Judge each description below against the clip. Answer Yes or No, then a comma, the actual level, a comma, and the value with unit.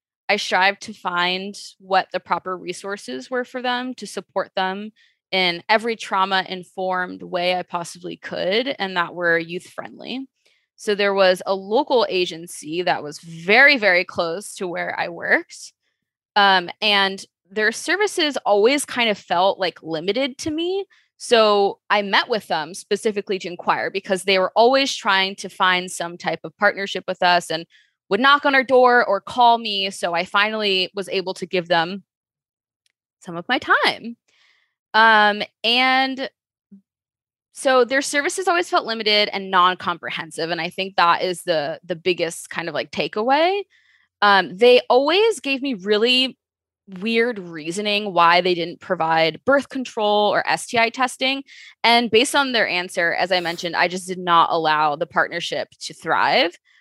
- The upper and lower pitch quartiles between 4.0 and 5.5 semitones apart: Yes, average, 5.2 semitones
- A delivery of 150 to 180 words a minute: Yes, average, 160 wpm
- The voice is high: Yes, high, 200 Hz